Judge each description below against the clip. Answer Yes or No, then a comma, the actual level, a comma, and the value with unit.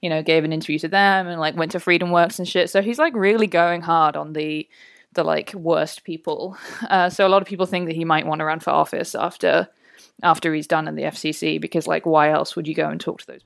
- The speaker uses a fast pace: Yes, fast, 270 wpm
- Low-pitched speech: No, medium, 165 Hz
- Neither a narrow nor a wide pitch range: Yes, average, 3.5 semitones